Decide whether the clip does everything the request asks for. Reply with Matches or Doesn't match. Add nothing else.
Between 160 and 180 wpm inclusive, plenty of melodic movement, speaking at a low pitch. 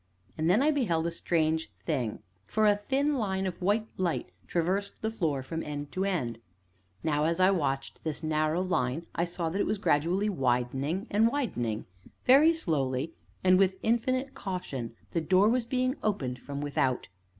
Doesn't match